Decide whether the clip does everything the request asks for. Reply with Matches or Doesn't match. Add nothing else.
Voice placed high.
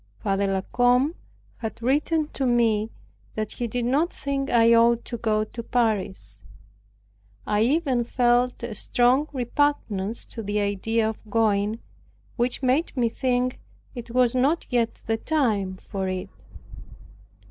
Matches